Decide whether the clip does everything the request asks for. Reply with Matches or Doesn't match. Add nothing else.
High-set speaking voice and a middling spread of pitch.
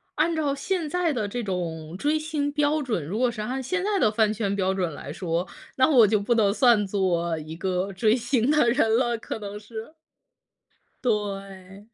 Doesn't match